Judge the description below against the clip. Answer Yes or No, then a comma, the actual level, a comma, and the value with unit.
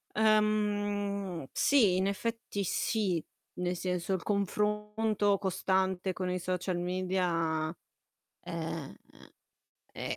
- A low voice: No, high, 190 Hz